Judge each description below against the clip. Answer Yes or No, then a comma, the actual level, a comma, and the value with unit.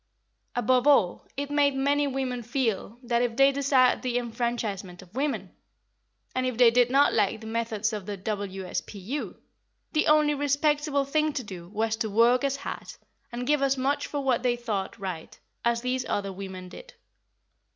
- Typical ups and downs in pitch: Yes, average, 4.5 semitones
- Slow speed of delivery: No, average, 170 wpm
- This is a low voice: No, high, 245 Hz